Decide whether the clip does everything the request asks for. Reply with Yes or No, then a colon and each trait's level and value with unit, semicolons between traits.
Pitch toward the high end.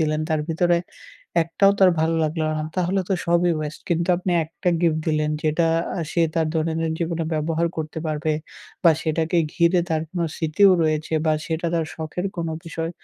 No: medium, 165 Hz